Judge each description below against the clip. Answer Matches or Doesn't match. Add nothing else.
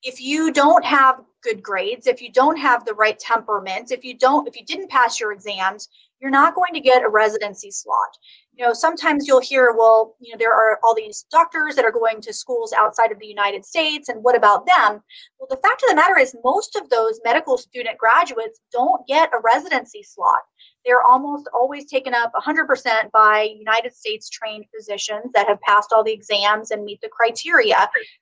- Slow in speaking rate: Doesn't match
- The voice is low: Doesn't match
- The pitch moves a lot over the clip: Matches